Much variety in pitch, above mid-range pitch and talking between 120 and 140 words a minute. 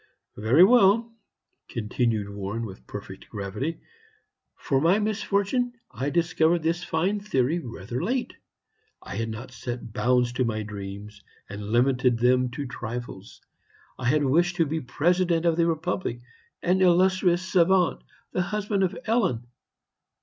No: wide, 7.5 semitones; medium, 145 Hz; slow, 135 wpm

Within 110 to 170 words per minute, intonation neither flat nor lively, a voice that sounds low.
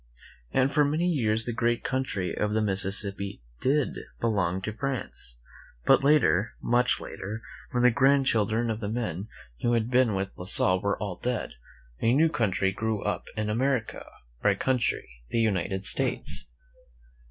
Yes: average, 160 wpm; average, 4.1 semitones; low, 110 Hz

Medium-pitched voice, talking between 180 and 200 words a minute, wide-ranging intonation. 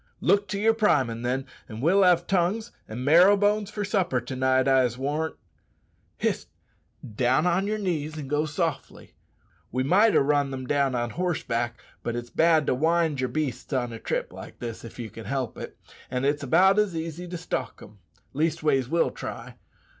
Yes: medium, 150 Hz; average, 185 wpm; wide, 5.7 semitones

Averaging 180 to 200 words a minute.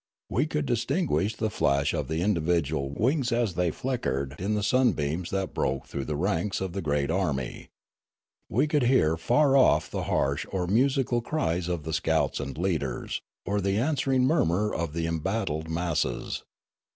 No: average, 165 wpm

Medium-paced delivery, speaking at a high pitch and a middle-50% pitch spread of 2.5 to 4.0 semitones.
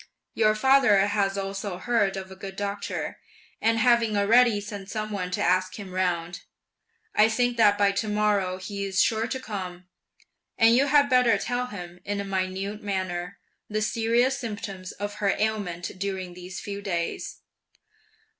Yes: average, 160 wpm; high, 205 Hz; average, 2.9 semitones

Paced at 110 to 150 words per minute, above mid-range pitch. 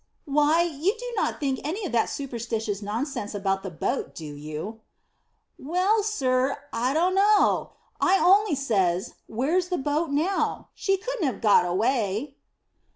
Yes: average, 145 wpm; very high, 275 Hz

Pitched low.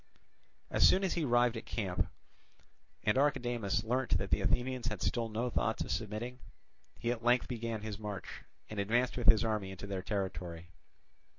Yes: low, 115 Hz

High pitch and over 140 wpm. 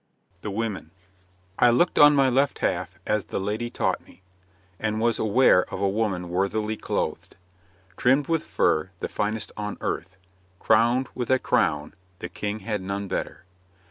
No: low, 105 Hz; average, 160 wpm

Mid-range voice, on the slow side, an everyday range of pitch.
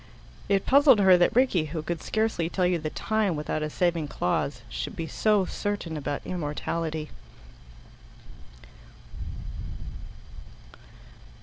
Yes: medium, 170 Hz; slow, 115 wpm; average, 4.7 semitones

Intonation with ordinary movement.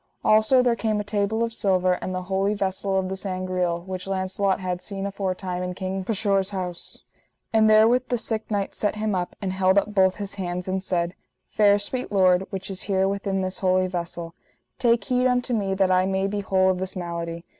No: narrow, 1.9 semitones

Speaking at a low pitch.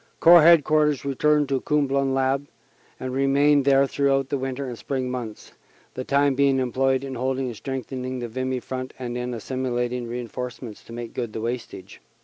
Yes: low, 130 Hz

